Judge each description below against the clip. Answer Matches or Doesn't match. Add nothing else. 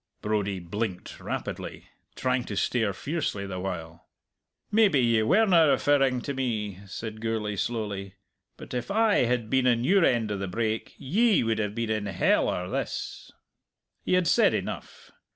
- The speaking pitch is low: Matches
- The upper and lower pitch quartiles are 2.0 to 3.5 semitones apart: Doesn't match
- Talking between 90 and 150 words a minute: Doesn't match